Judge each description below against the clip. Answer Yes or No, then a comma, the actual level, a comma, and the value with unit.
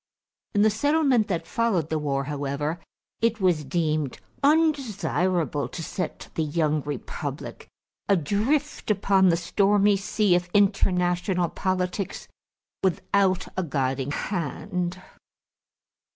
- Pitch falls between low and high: Yes, medium, 180 Hz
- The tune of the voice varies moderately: Yes, average, 4.7 semitones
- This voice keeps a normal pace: No, slow, 110 wpm